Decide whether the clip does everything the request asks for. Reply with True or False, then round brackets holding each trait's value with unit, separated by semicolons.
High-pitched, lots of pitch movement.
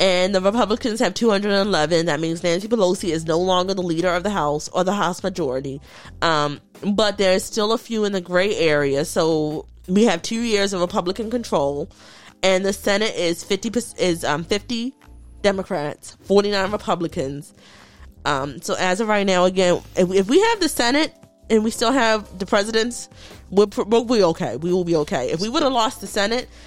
False (195 Hz; 4.2 semitones)